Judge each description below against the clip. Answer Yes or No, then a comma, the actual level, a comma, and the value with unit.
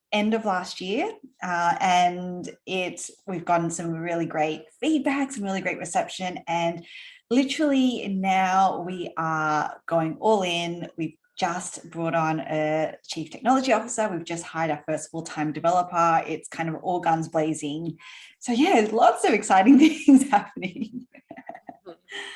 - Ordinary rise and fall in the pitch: No, wide, 5.9 semitones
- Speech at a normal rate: Yes, average, 145 wpm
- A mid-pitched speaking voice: Yes, medium, 180 Hz